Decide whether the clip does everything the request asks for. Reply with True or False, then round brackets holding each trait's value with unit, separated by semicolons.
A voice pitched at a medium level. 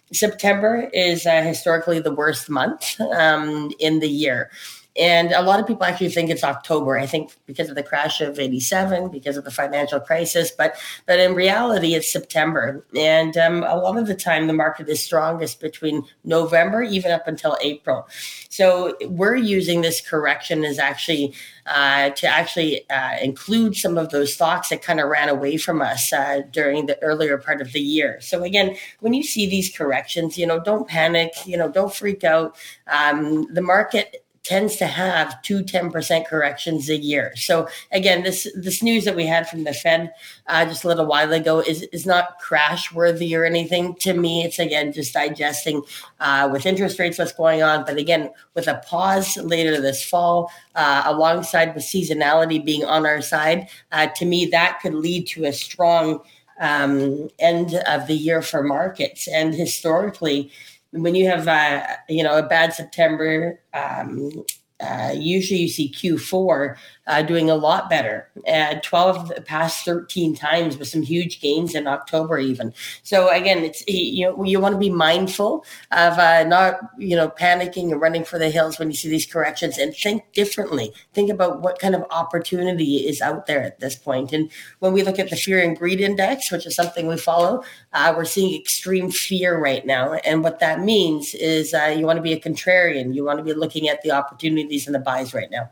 True (165 Hz)